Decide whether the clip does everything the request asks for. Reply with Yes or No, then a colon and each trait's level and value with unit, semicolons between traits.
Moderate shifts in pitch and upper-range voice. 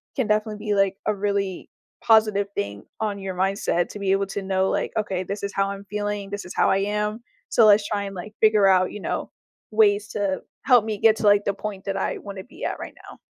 No: narrow, 1.4 semitones; high, 200 Hz